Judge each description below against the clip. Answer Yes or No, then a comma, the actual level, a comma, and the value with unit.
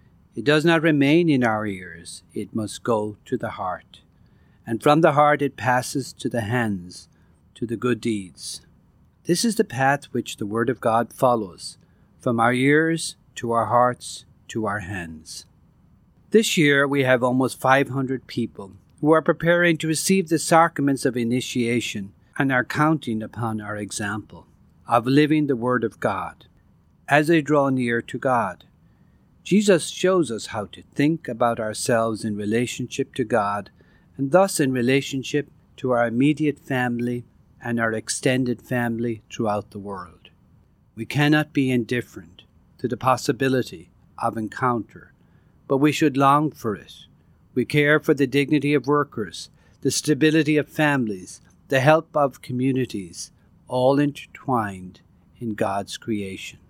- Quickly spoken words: No, average, 150 wpm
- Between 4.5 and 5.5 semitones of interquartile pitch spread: Yes, average, 4.8 semitones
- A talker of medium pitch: No, low, 125 Hz